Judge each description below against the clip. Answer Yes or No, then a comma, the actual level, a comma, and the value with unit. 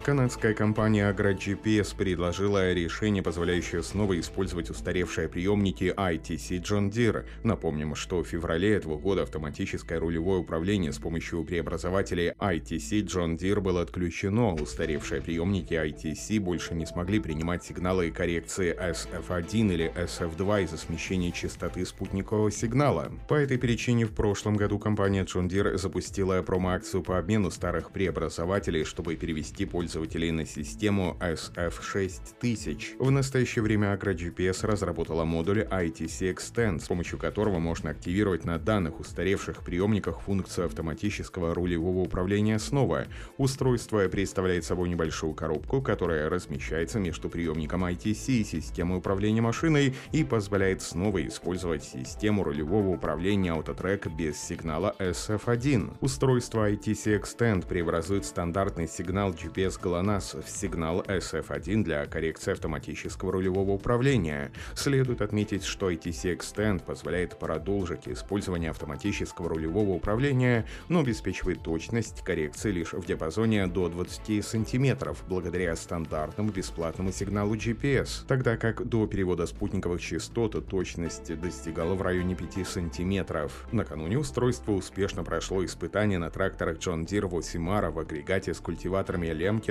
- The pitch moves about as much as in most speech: Yes, average, 4.0 semitones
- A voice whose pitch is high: No, very low, 95 Hz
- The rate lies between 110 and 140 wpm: Yes, average, 125 wpm